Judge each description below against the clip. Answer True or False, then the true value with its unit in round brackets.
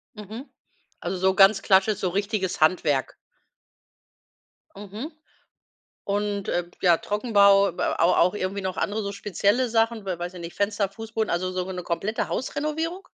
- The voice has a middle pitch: False (200 Hz)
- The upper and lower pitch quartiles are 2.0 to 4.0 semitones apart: True (2.8 semitones)